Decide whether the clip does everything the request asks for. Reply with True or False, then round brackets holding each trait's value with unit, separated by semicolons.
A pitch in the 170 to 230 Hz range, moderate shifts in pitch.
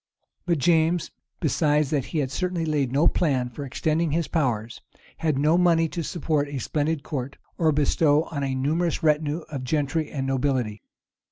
False (150 Hz; 3.0 semitones)